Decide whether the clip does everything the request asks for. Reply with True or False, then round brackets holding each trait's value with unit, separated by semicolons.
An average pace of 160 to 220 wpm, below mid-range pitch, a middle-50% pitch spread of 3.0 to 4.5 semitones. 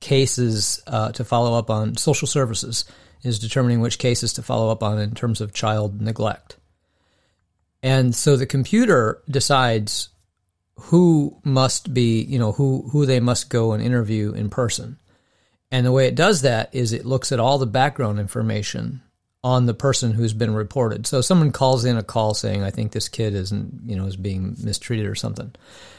True (180 wpm; 115 Hz; 3.6 semitones)